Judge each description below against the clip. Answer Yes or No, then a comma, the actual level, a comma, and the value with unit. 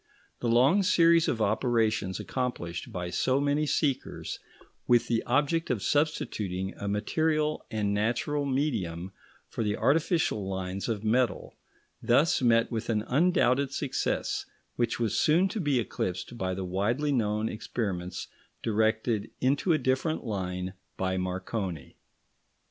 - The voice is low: Yes, low, 115 Hz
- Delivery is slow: Yes, slow, 130 wpm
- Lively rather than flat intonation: Yes, wide, 6.3 semitones